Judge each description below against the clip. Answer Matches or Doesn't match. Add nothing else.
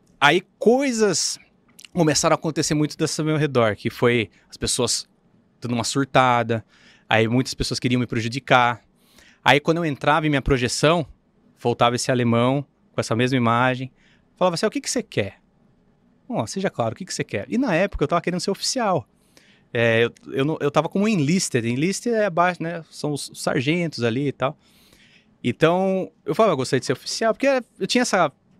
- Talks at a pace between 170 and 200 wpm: Matches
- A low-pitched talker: Doesn't match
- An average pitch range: Doesn't match